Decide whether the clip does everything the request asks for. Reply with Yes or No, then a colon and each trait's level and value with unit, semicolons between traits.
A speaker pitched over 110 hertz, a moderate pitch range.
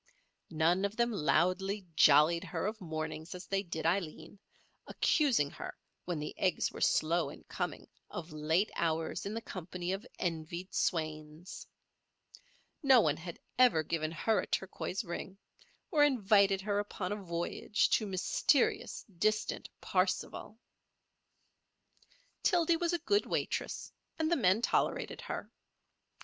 Yes: medium, 185 Hz; average, 4.5 semitones